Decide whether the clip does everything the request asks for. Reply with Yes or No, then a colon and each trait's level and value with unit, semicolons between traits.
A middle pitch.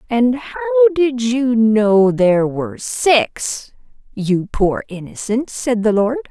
No: high, 240 Hz